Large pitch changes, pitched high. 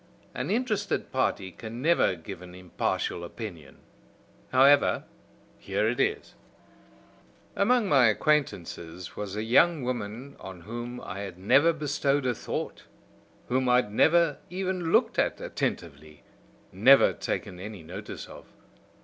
No: wide, 7.7 semitones; low, 120 Hz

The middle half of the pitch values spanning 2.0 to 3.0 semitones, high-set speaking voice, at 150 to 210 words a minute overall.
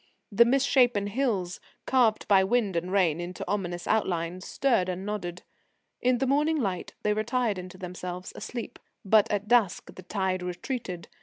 No: average, 4.7 semitones; high, 200 Hz; average, 155 wpm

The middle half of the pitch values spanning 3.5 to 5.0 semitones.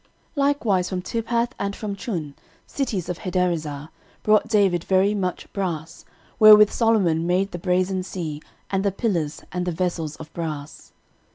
Yes: average, 3.8 semitones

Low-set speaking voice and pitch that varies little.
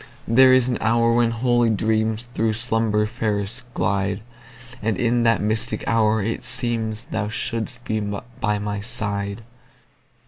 Yes: low, 115 Hz; narrow, 2.0 semitones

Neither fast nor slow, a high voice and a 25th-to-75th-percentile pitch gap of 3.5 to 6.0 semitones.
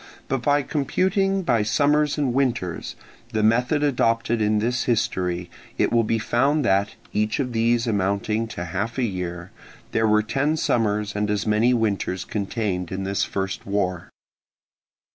No: average, 155 wpm; low, 110 Hz; average, 3.9 semitones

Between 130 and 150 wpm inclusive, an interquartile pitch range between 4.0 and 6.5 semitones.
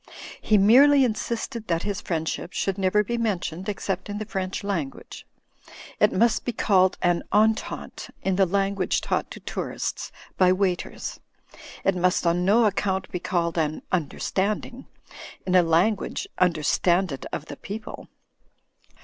No: average, 140 wpm; average, 3.0 semitones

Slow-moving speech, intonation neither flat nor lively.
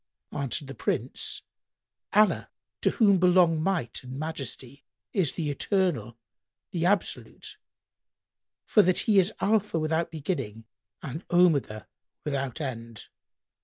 No: slow, 115 wpm; wide, 5.7 semitones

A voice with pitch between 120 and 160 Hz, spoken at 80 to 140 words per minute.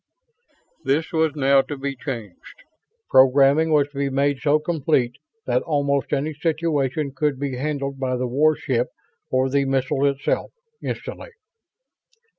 Yes: medium, 140 Hz; slow, 135 wpm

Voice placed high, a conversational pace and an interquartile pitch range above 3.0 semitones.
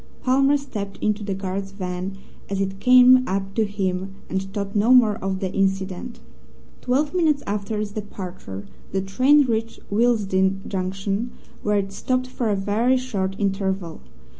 Yes: high, 200 Hz; average, 155 wpm; average, 3.8 semitones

